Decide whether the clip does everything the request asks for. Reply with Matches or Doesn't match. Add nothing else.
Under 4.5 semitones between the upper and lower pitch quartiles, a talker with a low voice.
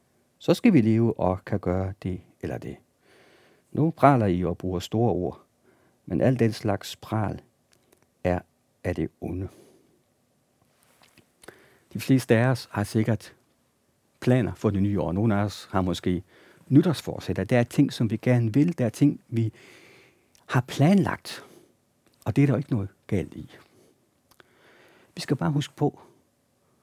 Doesn't match